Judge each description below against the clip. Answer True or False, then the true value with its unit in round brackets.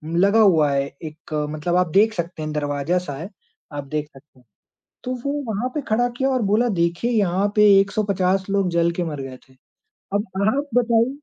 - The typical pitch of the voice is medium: True (180 Hz)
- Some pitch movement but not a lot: False (5.9 semitones)